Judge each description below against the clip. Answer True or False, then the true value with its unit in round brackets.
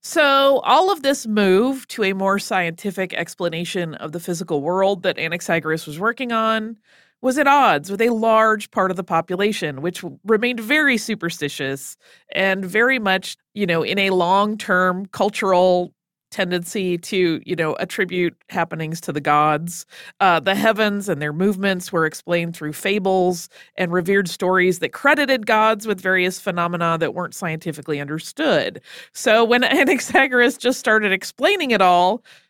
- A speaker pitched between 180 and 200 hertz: True (190 Hz)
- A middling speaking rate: True (155 wpm)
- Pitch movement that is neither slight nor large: True (4.3 semitones)